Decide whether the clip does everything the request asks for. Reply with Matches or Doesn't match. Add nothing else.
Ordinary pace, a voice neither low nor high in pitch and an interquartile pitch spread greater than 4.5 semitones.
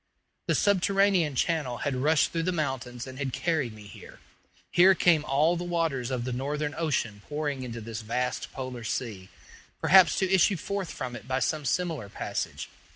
Matches